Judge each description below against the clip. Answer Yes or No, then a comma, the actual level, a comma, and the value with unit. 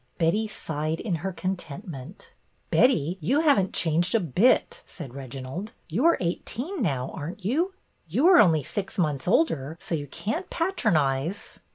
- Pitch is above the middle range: No, medium, 175 Hz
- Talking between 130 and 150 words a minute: No, average, 175 wpm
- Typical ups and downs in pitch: No, wide, 6.6 semitones